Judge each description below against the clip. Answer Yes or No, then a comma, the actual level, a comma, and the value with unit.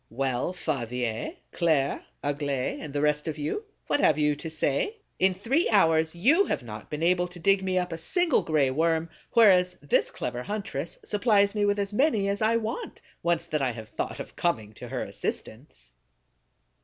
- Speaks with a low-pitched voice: No, medium, 165 Hz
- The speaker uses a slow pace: No, average, 185 wpm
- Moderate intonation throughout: No, wide, 5.9 semitones